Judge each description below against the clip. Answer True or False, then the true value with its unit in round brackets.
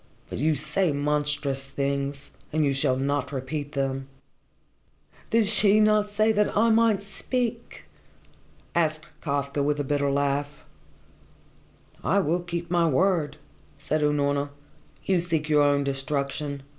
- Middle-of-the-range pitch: True (150 Hz)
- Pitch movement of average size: True (4.1 semitones)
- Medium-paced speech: False (130 wpm)